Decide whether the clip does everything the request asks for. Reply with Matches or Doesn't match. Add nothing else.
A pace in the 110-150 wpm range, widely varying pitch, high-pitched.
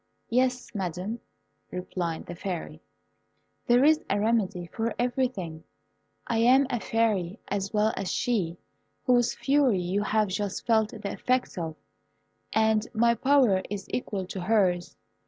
Doesn't match